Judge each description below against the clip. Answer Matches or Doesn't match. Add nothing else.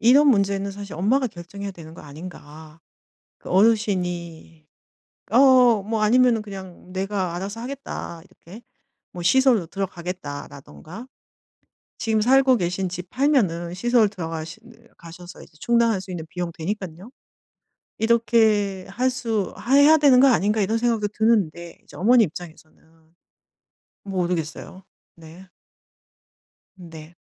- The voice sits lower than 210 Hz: Matches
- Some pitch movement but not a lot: Matches